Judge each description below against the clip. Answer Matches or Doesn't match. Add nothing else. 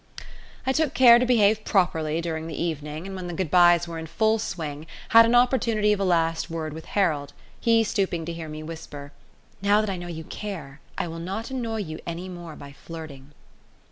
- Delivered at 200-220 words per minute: Matches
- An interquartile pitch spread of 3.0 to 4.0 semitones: Doesn't match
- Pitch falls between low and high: Matches